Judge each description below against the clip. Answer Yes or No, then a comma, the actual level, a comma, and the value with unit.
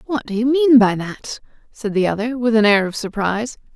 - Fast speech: Yes, fast, 225 wpm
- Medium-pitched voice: No, high, 230 Hz